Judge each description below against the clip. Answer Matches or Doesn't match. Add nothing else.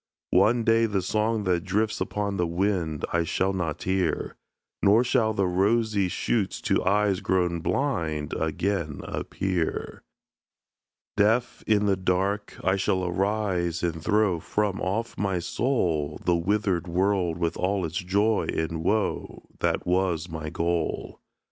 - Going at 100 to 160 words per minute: Matches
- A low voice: Matches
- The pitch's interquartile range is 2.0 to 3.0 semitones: Doesn't match